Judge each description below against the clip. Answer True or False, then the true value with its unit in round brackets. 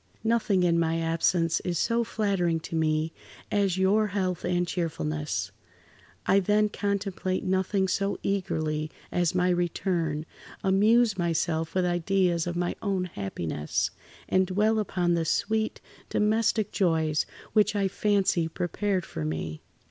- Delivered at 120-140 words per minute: True (135 wpm)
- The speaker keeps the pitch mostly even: False (3.4 semitones)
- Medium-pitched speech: True (180 Hz)